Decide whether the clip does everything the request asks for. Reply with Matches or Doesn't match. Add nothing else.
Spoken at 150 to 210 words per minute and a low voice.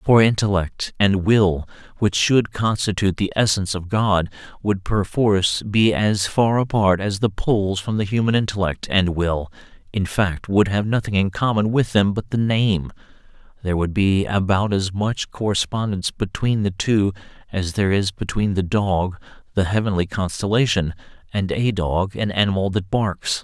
Matches